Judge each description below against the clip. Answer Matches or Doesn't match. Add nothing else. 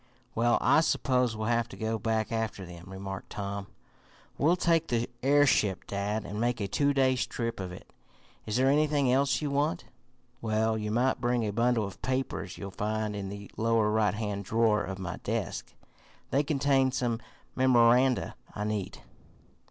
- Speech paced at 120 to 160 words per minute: Doesn't match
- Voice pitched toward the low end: Matches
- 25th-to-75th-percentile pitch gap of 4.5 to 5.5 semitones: Doesn't match